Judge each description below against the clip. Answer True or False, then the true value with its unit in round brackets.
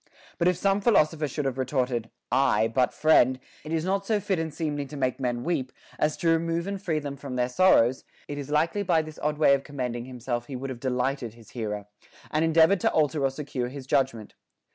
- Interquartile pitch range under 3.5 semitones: False (4.2 semitones)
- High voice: False (140 Hz)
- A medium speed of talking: False (220 wpm)